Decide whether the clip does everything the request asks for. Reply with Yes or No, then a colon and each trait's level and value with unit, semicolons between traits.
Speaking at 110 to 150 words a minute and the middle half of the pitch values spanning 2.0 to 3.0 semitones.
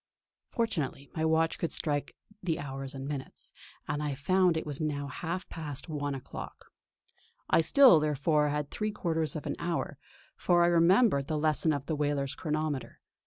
No: average, 165 wpm; average, 2.7 semitones